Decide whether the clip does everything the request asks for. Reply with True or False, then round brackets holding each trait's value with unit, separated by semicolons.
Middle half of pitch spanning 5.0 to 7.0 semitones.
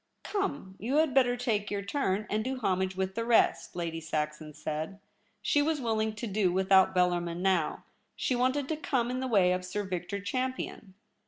True (5.5 semitones)